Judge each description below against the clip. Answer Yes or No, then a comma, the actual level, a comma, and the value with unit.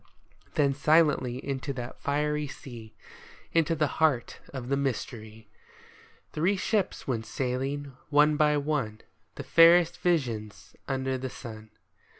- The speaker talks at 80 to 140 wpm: Yes, slow, 135 wpm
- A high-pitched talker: No, medium, 140 Hz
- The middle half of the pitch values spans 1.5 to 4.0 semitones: Yes, average, 3.6 semitones